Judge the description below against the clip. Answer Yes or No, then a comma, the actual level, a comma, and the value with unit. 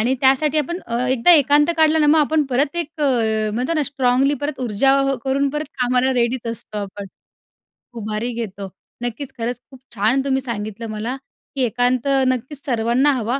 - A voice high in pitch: Yes, very high, 255 Hz